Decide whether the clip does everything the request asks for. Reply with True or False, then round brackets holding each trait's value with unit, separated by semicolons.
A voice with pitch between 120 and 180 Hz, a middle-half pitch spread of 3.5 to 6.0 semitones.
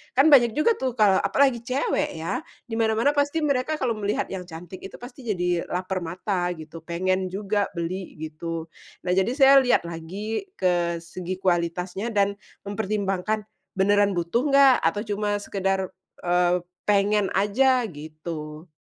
False (195 Hz; 4.6 semitones)